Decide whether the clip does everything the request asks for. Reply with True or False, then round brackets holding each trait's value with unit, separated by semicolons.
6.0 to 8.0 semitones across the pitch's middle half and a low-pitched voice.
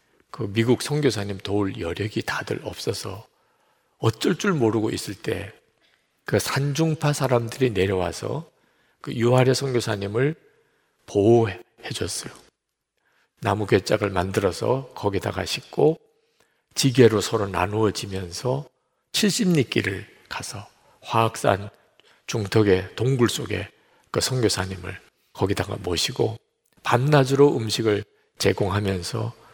False (5.2 semitones; 115 Hz)